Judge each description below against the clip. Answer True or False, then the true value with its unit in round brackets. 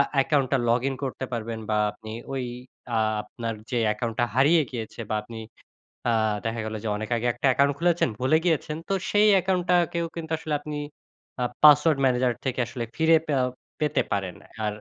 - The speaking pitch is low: True (130 Hz)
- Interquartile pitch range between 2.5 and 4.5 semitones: False (5.3 semitones)